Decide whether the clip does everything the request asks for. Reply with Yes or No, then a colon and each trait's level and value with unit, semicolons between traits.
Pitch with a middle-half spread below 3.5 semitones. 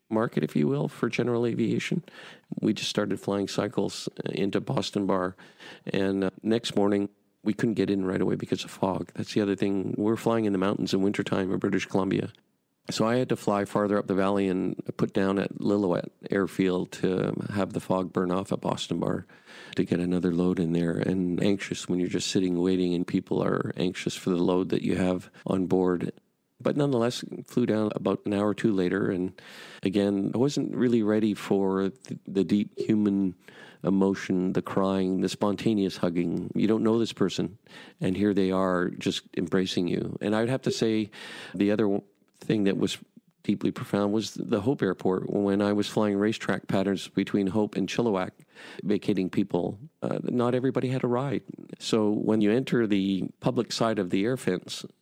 Yes: narrow, 2.4 semitones